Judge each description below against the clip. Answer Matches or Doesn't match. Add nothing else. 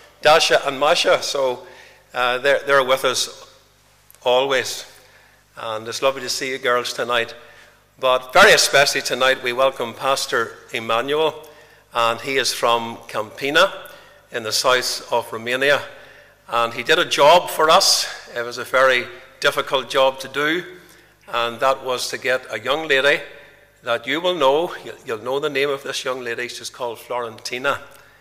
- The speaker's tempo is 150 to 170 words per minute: Matches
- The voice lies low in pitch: Matches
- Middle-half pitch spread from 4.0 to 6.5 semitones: Doesn't match